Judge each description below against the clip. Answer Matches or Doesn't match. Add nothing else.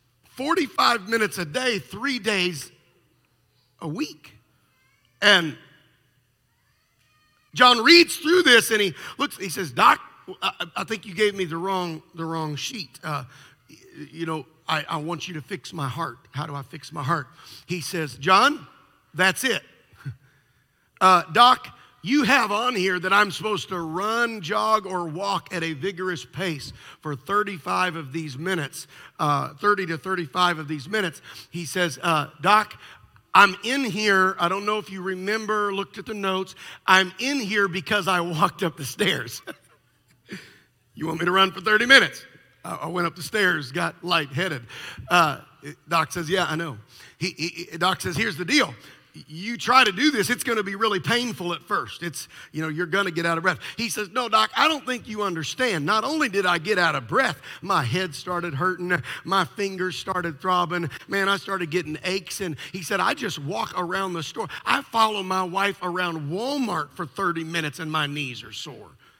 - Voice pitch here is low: Doesn't match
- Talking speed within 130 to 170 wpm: Doesn't match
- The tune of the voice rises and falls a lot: Doesn't match